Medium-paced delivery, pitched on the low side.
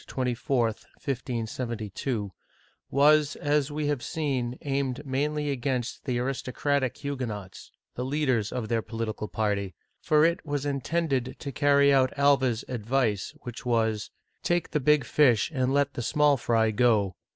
Yes: average, 145 wpm; low, 130 Hz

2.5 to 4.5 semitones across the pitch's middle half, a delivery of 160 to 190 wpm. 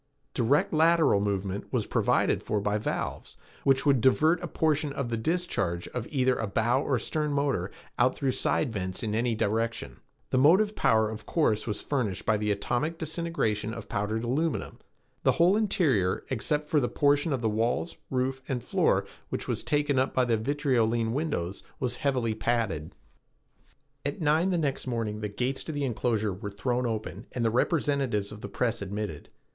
No: average, 5.2 semitones; average, 175 wpm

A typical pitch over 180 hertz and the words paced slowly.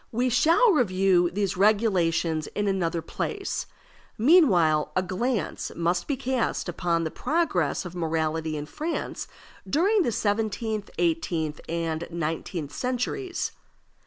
Yes: high, 190 Hz; slow, 120 wpm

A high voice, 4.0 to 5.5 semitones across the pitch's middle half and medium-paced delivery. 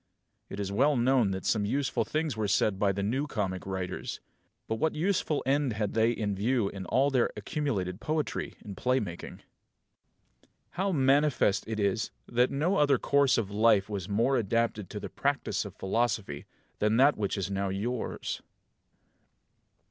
No: low, 115 Hz; average, 5.2 semitones; average, 165 wpm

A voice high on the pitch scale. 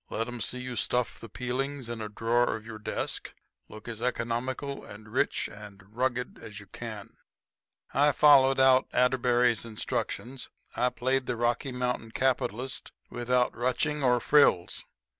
No: low, 125 Hz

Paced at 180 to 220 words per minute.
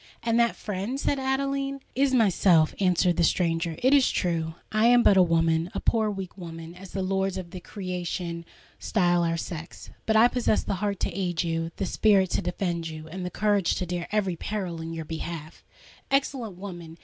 Yes: average, 185 wpm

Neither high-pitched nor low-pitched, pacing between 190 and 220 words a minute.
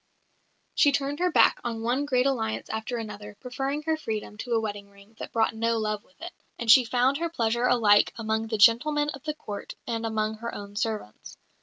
No: high, 230 Hz; fast, 205 wpm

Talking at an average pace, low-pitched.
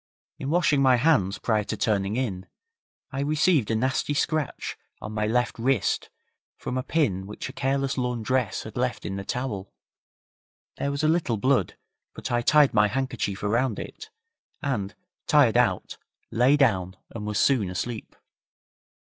Yes: average, 155 wpm; low, 125 Hz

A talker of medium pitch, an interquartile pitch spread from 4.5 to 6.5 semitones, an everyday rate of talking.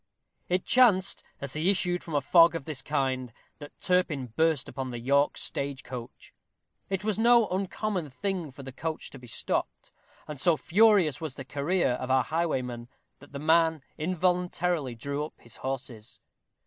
Yes: medium, 155 Hz; average, 5.2 semitones; average, 170 wpm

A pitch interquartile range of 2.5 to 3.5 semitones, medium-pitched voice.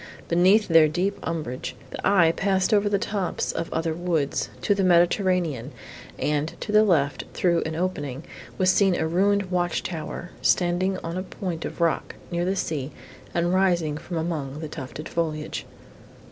Yes: average, 2.9 semitones; medium, 175 Hz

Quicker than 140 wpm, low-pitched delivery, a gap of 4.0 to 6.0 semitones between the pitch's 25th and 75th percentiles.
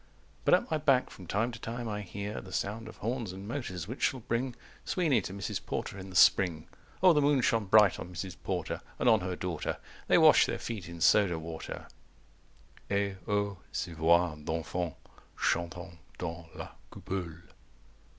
Yes: average, 180 wpm; low, 100 Hz; average, 4.7 semitones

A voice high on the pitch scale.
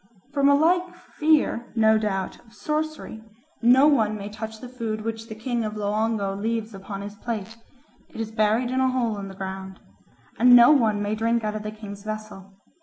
Yes: high, 220 Hz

